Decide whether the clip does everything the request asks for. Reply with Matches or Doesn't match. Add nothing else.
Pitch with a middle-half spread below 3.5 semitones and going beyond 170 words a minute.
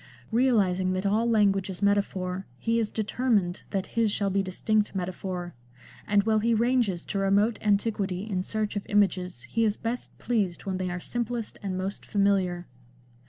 Doesn't match